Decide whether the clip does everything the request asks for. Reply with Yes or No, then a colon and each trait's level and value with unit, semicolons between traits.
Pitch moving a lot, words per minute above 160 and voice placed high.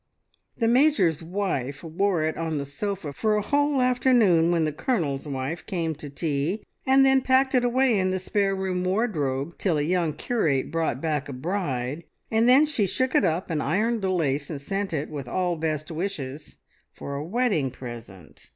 No: wide, 6.3 semitones; average, 190 wpm; medium, 170 Hz